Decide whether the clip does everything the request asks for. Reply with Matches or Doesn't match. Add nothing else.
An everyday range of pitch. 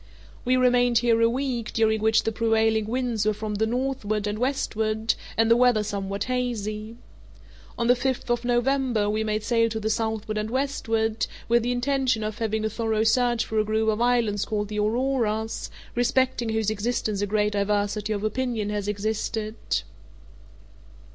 Doesn't match